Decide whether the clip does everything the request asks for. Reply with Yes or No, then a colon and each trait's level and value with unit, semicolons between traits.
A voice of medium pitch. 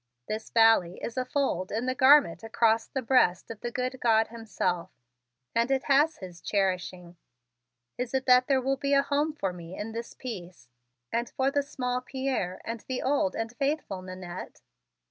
No: high, 235 Hz